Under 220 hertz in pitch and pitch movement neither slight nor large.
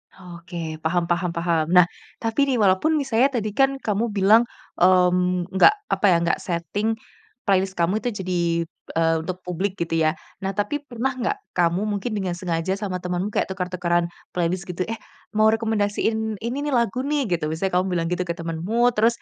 Yes: medium, 185 Hz; average, 4.1 semitones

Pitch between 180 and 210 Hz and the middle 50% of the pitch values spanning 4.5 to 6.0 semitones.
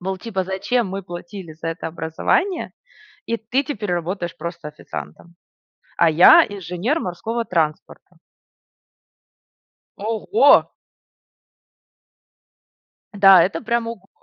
Yes: high, 190 Hz; average, 5.0 semitones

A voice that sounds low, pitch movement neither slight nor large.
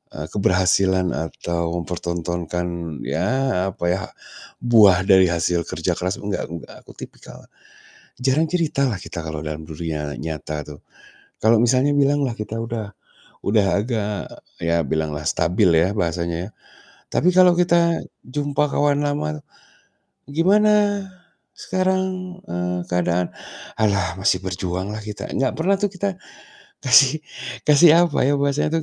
No: low, 105 Hz; wide, 8.9 semitones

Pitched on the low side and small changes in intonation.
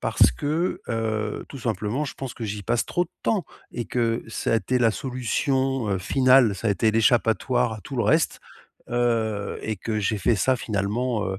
No: low, 115 Hz; average, 3.2 semitones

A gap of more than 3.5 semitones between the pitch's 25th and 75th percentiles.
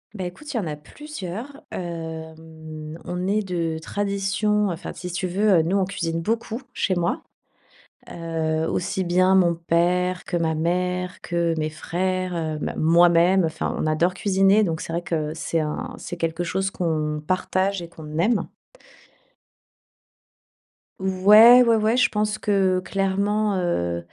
No: average, 3.1 semitones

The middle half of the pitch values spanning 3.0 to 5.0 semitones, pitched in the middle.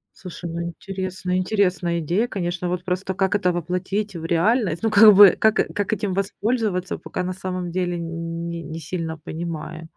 No: narrow, 2.5 semitones; medium, 180 Hz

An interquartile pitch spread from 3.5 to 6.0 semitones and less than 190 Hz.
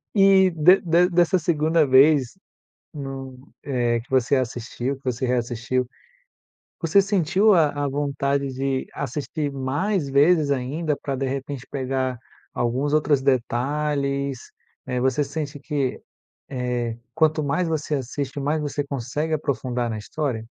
No: average, 3.0 semitones; medium, 140 Hz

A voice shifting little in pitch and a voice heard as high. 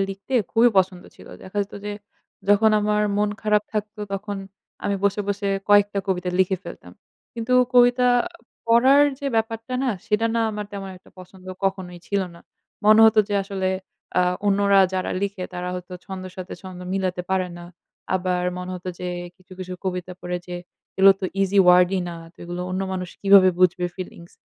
Yes: narrow, 2.3 semitones; high, 195 Hz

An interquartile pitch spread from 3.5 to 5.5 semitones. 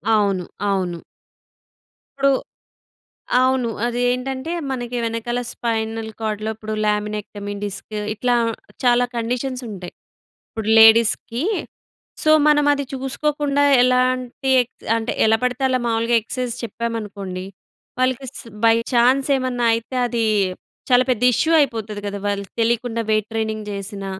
No: average, 3.0 semitones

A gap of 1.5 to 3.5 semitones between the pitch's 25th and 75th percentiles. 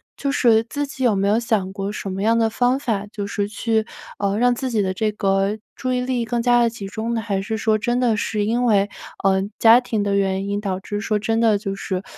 Yes: average, 2.8 semitones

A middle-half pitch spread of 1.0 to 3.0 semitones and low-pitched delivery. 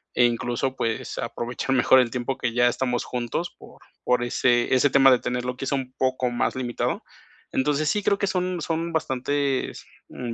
Yes: narrow, 2.5 semitones; low, 130 Hz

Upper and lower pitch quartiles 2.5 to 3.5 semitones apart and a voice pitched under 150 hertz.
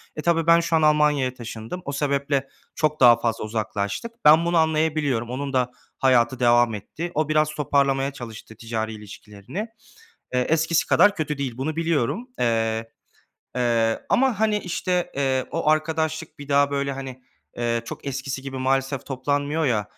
No: average, 4.5 semitones; medium, 140 Hz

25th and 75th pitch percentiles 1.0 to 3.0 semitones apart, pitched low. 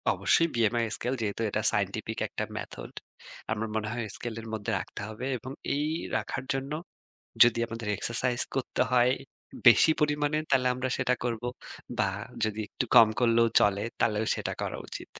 Yes: narrow, 2.5 semitones; low, 115 Hz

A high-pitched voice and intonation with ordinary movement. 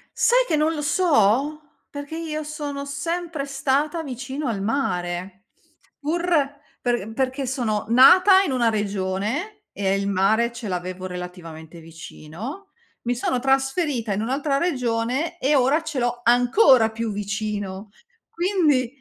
No: very high, 255 Hz; wide, 6.2 semitones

